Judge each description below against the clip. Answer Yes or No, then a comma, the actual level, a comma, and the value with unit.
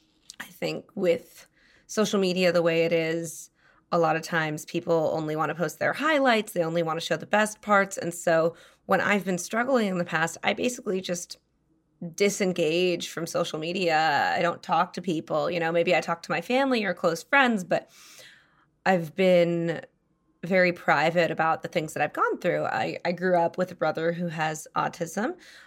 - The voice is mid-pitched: Yes, medium, 170 Hz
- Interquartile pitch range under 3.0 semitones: Yes, narrow, 2.4 semitones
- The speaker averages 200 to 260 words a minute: No, average, 190 wpm